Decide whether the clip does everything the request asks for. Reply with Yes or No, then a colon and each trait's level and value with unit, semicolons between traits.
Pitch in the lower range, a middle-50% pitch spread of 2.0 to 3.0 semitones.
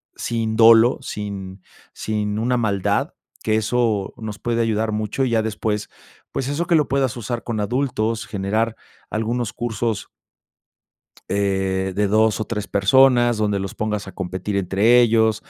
Yes: low, 110 Hz; narrow, 2.4 semitones